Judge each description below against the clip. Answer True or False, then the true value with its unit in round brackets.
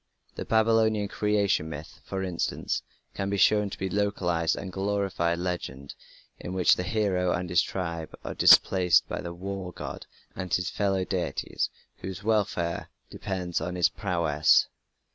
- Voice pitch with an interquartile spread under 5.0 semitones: True (2.6 semitones)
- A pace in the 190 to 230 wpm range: False (155 wpm)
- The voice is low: True (90 Hz)